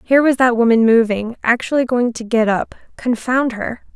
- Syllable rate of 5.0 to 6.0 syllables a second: Yes, 5.1 syllables/s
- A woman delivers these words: Yes, female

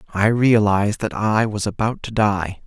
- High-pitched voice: No, low, 105 Hz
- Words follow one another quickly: No, average, 180 wpm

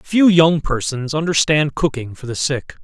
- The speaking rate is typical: Yes, average, 170 wpm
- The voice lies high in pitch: No, medium, 150 Hz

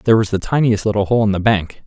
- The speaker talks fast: Yes, fast, 290 wpm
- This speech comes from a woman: No, male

